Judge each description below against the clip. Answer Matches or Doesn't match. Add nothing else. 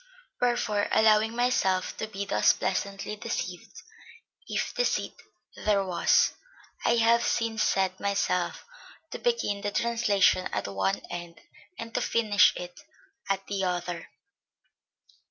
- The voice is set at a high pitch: Matches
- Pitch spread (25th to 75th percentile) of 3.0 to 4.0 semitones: Matches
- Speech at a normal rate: Doesn't match